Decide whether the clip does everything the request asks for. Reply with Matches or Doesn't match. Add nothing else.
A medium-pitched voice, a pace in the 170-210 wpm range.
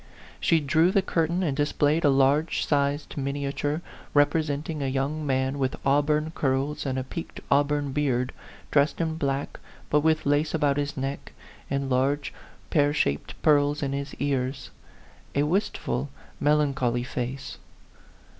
Doesn't match